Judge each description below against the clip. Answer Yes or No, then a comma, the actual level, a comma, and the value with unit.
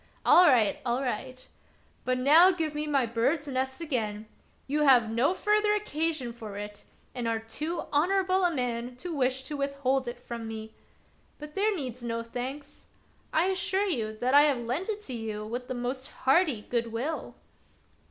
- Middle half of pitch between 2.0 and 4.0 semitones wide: No, average, 4.7 semitones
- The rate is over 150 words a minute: Yes, average, 170 wpm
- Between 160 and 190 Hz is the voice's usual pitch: No, very high, 260 Hz